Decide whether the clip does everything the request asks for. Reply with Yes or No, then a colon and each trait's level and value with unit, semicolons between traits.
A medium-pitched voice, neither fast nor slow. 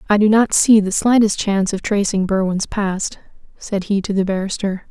No: high, 200 Hz; average, 195 wpm